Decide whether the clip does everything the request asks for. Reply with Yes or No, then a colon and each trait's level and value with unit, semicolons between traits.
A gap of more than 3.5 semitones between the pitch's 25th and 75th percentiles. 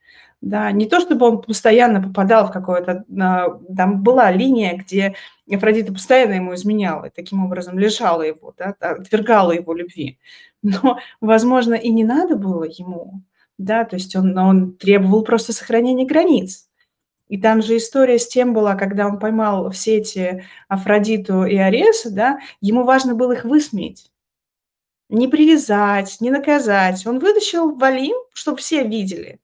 Yes: average, 4.8 semitones